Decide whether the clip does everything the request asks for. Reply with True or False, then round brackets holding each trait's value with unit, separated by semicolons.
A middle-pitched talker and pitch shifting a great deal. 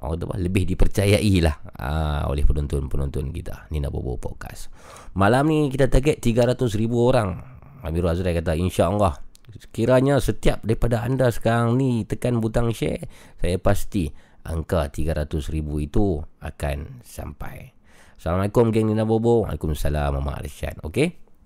False (95 Hz; 7.5 semitones)